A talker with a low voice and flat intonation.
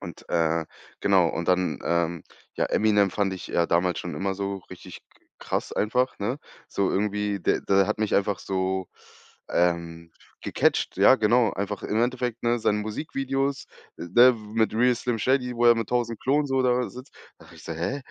No: low, 105 Hz; average, 4.8 semitones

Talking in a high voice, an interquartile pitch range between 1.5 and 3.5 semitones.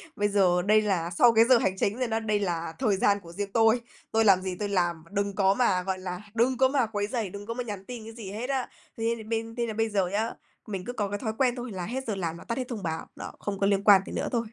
Yes: high, 205 Hz; average, 3.2 semitones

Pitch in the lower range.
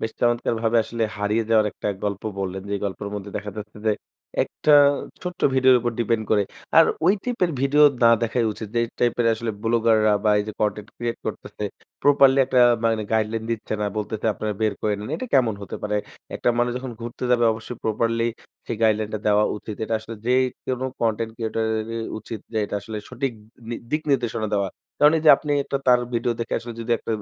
Yes: low, 115 Hz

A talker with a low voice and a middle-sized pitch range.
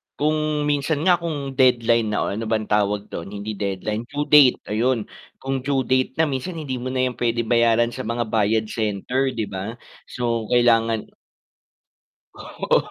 Yes: low, 120 Hz; average, 3.6 semitones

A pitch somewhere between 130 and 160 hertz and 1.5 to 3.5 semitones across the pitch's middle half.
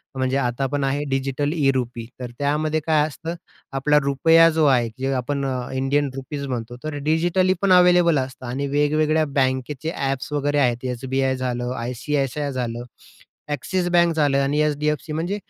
Yes: medium, 140 Hz; average, 2.8 semitones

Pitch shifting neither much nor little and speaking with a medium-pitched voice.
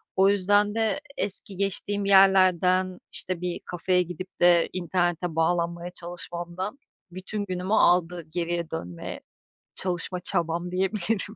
No: narrow, 2.0 semitones; medium, 180 Hz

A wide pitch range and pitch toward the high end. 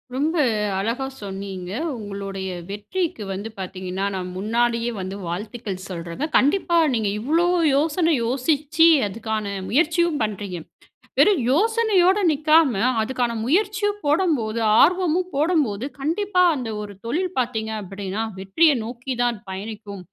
Yes: wide, 8.3 semitones; high, 240 Hz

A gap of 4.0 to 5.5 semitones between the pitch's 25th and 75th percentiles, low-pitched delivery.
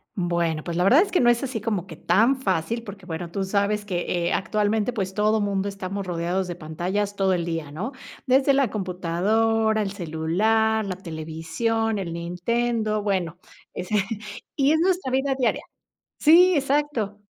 No: average, 4.3 semitones; high, 205 Hz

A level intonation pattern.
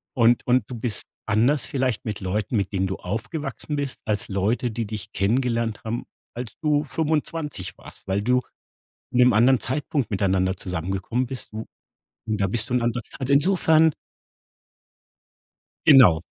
No: average, 4.5 semitones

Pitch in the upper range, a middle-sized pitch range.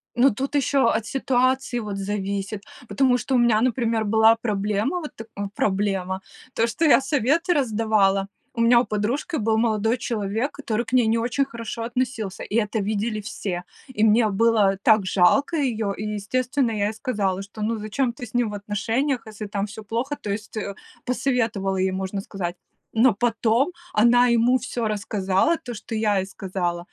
Yes: high, 220 Hz; average, 3.2 semitones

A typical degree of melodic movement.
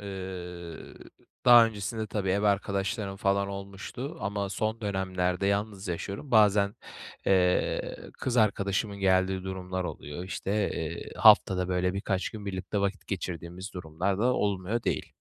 No: narrow, 1.8 semitones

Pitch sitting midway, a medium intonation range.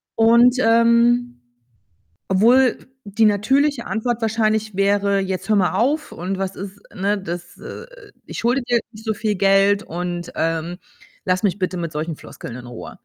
No: high, 205 Hz; average, 4.0 semitones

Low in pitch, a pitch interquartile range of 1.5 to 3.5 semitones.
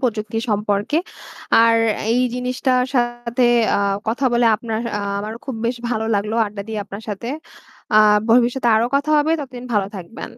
No: high, 230 Hz; average, 2.8 semitones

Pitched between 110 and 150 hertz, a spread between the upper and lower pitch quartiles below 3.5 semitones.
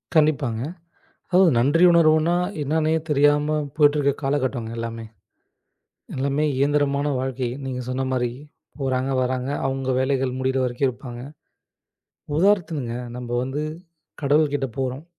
Yes: low, 135 Hz; narrow, 2.6 semitones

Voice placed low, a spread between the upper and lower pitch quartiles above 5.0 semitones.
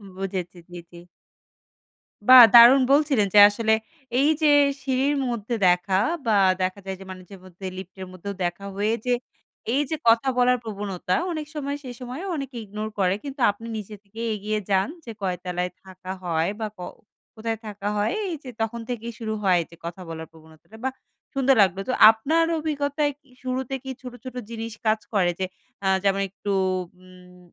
No: high, 215 Hz; wide, 5.5 semitones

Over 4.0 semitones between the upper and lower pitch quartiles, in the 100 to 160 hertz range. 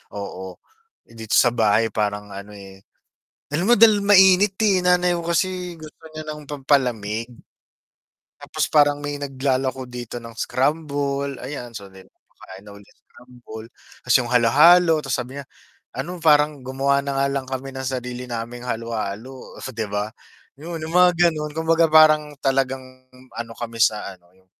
Yes: average, 4.8 semitones; low, 135 Hz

